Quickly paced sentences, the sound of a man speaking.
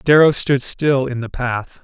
No: average, 195 wpm; male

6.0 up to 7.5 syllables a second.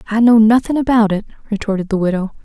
Yes: 6.8 syllables/s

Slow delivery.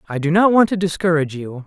No: fast, 250 wpm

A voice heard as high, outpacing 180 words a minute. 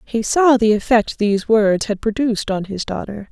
Yes: high, 220 Hz; average, 200 wpm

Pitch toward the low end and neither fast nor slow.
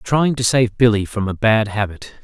No: low, 110 Hz; fast, 215 wpm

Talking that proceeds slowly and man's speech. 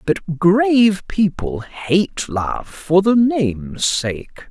Yes: slow, 120 wpm; male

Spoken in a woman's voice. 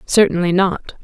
Yes: female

